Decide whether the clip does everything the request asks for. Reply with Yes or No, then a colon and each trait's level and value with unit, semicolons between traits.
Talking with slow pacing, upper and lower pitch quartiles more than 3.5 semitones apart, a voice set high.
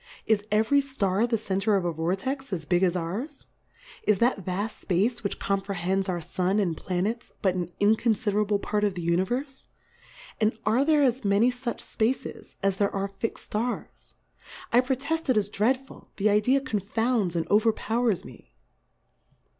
No: average, 170 wpm; average, 4.1 semitones; high, 210 Hz